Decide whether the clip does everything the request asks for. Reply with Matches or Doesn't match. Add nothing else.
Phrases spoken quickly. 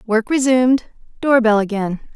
Doesn't match